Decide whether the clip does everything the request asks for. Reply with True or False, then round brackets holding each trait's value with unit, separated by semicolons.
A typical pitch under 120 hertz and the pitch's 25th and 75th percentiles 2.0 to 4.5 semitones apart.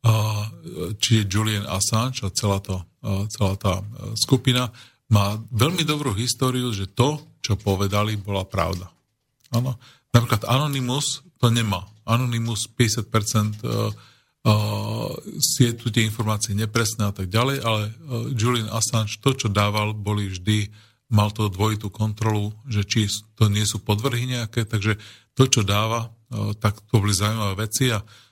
True (110 Hz; 2.5 semitones)